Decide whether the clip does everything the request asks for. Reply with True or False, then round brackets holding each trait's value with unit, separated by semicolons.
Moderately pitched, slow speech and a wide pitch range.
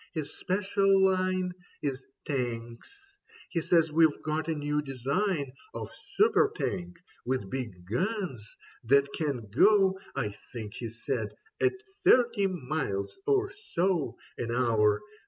True (155 Hz; 125 wpm; 7.4 semitones)